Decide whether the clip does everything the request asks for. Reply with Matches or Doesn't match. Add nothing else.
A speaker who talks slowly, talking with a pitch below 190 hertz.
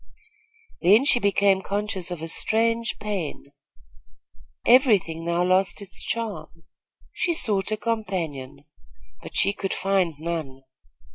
Doesn't match